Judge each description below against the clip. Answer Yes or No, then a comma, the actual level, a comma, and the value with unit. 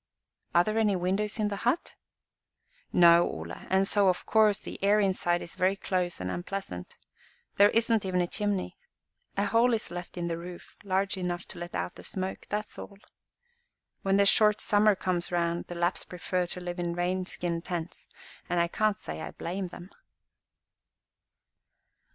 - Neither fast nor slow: Yes, average, 175 wpm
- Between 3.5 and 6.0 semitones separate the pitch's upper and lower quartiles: No, average, 2.7 semitones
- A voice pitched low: No, medium, 185 Hz